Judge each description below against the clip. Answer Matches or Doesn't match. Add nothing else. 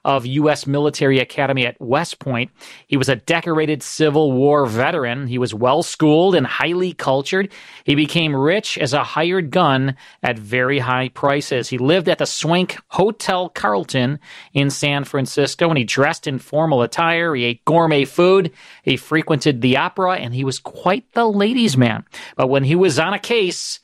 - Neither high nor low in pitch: Matches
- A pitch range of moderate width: Matches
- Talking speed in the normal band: Matches